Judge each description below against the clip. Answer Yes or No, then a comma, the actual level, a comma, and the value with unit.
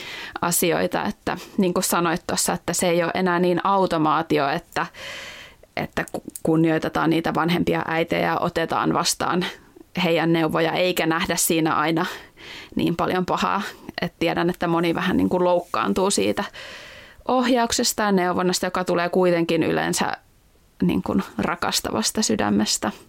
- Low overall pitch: No, medium, 175 Hz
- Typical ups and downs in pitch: No, narrow, 1.8 semitones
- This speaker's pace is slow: No, average, 130 wpm